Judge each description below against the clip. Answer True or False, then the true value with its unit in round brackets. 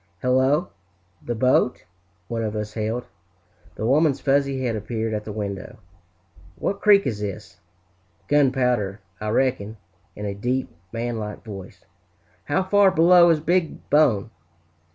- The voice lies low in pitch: True (120 Hz)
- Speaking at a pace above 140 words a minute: False (135 wpm)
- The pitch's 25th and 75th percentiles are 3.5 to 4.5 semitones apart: False (5.4 semitones)